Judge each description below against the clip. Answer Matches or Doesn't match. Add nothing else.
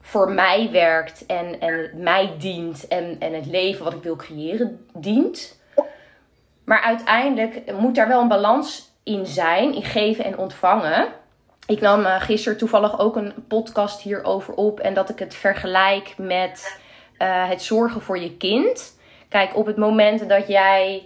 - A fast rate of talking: Doesn't match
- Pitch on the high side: Matches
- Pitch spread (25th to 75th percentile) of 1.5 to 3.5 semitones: Matches